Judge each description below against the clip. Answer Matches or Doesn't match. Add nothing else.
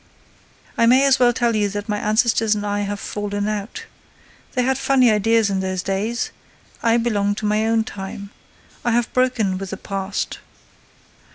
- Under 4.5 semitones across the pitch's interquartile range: Matches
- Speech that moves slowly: Doesn't match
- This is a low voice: Doesn't match